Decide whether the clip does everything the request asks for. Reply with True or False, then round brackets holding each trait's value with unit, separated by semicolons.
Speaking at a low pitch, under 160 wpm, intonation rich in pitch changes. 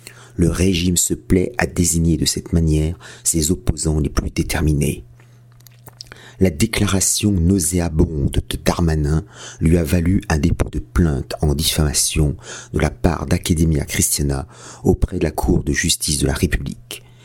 False (85 Hz; 145 wpm; 3.8 semitones)